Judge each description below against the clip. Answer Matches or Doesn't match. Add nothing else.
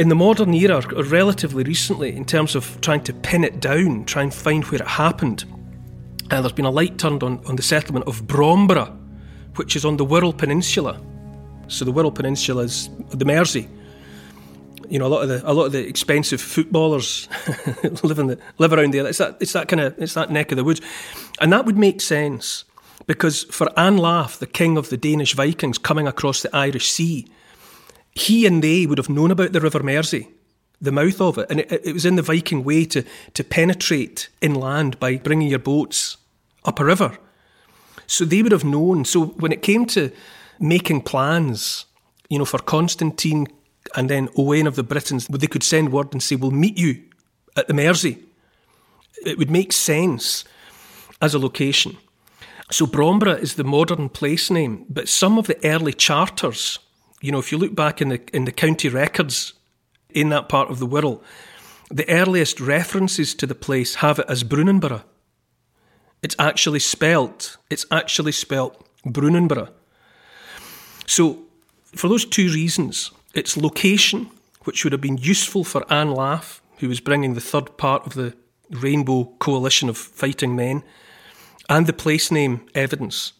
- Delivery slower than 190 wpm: Matches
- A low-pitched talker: Doesn't match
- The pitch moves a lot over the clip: Doesn't match